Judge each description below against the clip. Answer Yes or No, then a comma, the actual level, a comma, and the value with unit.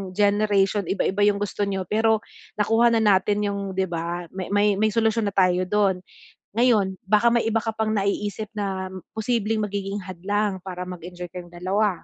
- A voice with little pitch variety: Yes, narrow, 2.2 semitones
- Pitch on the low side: No, high, 205 Hz